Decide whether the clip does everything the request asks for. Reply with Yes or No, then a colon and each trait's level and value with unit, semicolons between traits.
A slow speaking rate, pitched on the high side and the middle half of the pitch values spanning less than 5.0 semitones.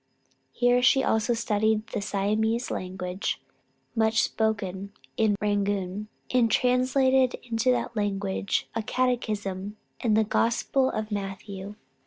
Yes: slow, 115 wpm; high, 215 Hz; average, 3.0 semitones